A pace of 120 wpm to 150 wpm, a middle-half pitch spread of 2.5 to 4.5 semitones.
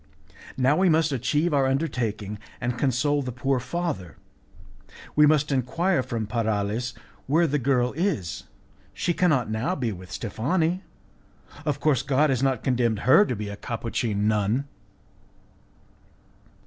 No: slow, 135 wpm; average, 4.9 semitones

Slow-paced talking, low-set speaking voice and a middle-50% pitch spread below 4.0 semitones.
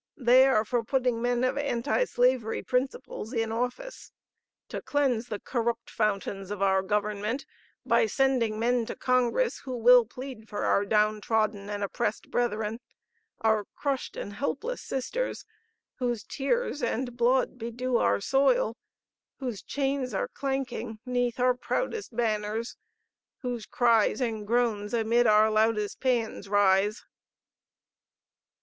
No: slow, 130 wpm; high, 235 Hz; average, 3.1 semitones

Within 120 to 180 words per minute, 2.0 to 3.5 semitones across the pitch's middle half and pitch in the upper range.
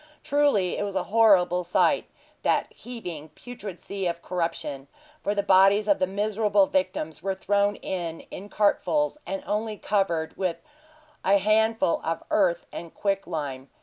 Yes: average, 150 wpm; average, 3.2 semitones; high, 195 Hz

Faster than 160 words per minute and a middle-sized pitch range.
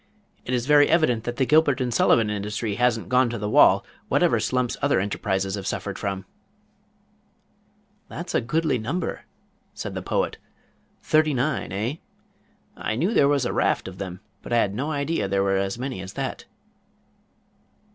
No: average, 175 wpm; wide, 6.1 semitones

